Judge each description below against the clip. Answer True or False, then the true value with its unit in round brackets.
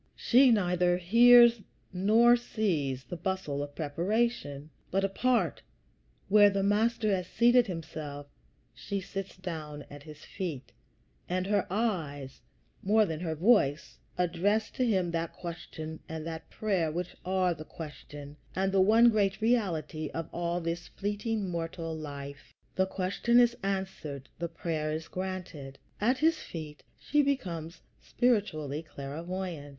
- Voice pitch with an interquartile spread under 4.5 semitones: False (4.9 semitones)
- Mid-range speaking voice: True (180 Hz)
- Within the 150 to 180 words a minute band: False (135 wpm)